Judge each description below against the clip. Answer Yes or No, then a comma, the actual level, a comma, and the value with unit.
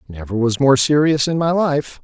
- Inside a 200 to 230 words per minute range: Yes, fast, 205 wpm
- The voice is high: No, medium, 140 Hz